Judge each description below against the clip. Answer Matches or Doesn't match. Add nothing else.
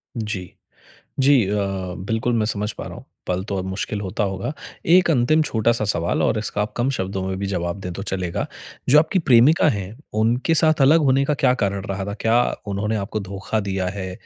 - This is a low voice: Matches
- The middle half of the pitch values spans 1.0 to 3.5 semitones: Doesn't match